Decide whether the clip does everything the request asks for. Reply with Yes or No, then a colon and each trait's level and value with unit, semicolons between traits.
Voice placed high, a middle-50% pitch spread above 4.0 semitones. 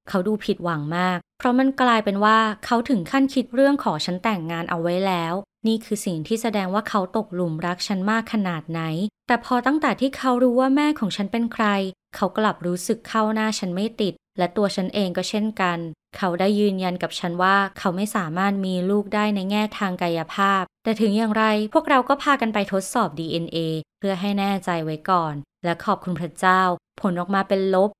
No: high, 200 Hz; average, 3.6 semitones